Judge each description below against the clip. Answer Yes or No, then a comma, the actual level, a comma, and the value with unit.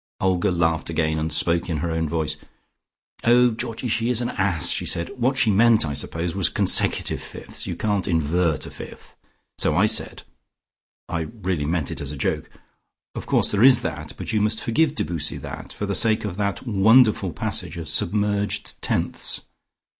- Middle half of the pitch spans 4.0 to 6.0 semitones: Yes, average, 5.2 semitones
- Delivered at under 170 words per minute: No, average, 185 wpm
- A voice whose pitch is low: Yes, very low, 95 Hz